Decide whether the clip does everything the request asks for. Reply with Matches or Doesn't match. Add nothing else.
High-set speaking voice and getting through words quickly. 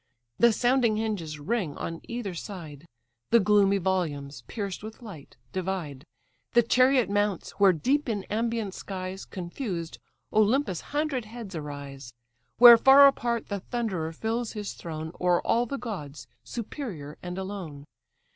Doesn't match